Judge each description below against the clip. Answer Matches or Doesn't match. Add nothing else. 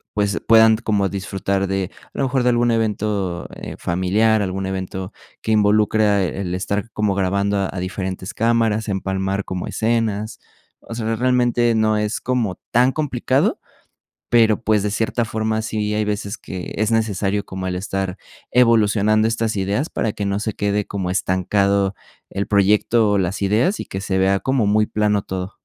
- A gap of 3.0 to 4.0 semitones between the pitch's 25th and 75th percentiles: Doesn't match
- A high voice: Doesn't match